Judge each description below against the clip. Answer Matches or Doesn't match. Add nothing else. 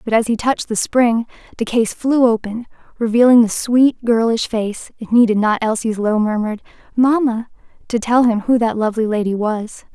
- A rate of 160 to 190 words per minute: Matches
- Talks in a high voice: Matches